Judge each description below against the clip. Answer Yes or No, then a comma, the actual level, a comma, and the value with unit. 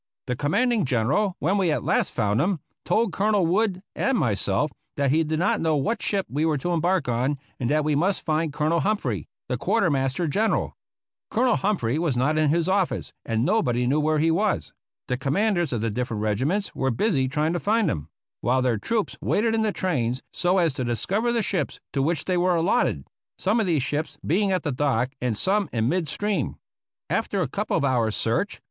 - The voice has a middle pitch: Yes, medium, 155 Hz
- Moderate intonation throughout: No, wide, 6.9 semitones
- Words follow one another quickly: Yes, fast, 215 wpm